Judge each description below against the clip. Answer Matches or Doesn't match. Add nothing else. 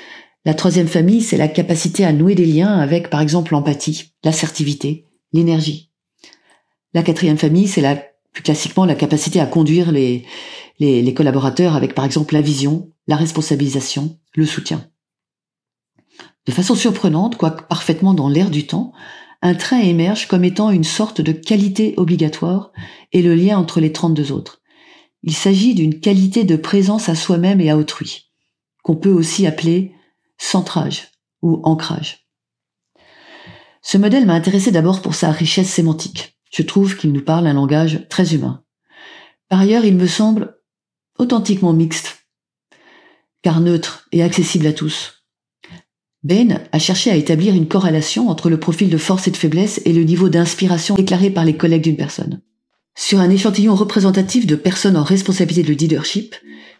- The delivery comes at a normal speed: Matches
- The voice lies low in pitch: Doesn't match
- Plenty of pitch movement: Doesn't match